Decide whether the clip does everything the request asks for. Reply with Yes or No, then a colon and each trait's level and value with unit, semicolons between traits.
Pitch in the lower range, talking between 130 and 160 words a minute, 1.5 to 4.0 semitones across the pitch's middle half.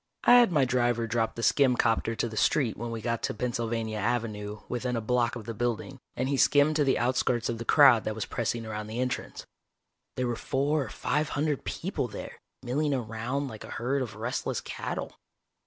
No: low, 120 Hz; fast, 205 wpm; average, 2.9 semitones